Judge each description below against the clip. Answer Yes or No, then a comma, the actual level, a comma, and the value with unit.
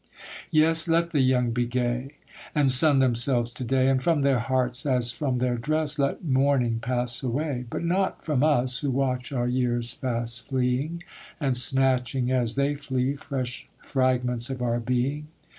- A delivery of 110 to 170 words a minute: Yes, average, 165 wpm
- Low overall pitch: Yes, low, 130 Hz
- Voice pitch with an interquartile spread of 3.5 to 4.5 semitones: No, narrow, 2.4 semitones